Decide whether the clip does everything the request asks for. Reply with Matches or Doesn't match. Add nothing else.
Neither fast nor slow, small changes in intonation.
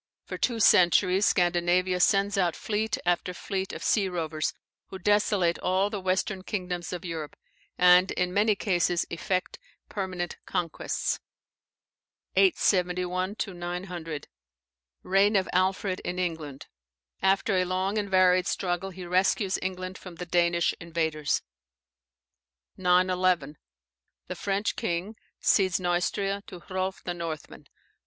Doesn't match